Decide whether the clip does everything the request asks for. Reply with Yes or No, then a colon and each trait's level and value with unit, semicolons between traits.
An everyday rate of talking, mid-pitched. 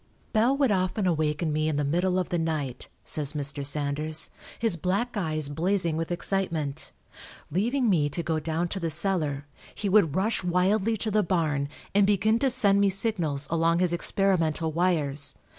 Yes: average, 175 wpm; medium, 170 Hz